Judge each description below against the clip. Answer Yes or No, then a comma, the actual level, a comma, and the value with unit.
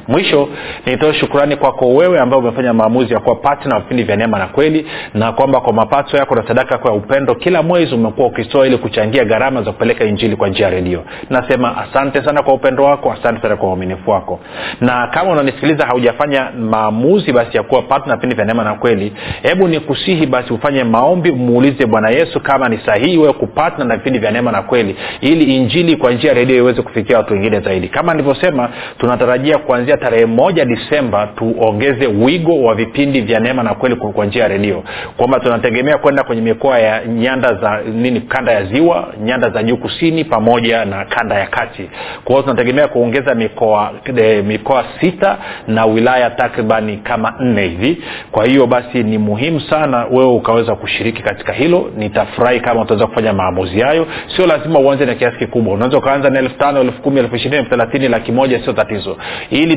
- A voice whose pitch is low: Yes, low, 125 Hz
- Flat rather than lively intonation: No, average, 3.9 semitones